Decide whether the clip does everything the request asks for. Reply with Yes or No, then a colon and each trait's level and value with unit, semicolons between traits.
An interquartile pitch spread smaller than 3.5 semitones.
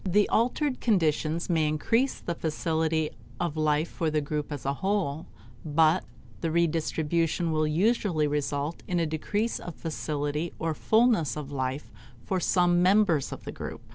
Yes: average, 2.9 semitones